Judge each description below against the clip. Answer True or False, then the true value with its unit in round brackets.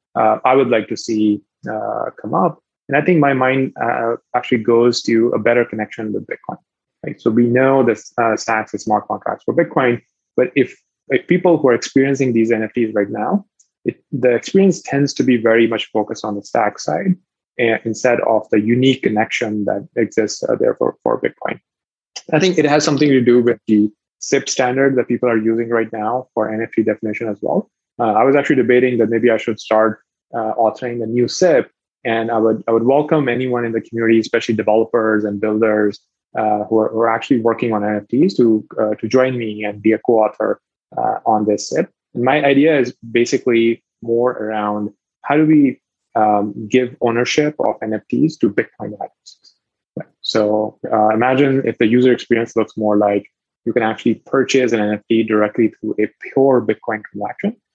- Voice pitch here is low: True (115 Hz)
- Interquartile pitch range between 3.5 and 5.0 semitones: False (2.9 semitones)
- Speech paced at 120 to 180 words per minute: False (190 wpm)